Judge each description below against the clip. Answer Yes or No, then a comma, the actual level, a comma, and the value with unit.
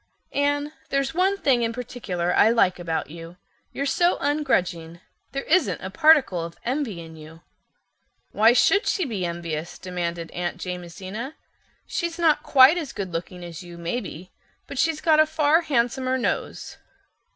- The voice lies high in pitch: Yes, high, 230 Hz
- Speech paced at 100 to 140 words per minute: No, average, 150 wpm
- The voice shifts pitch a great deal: Yes, wide, 9.0 semitones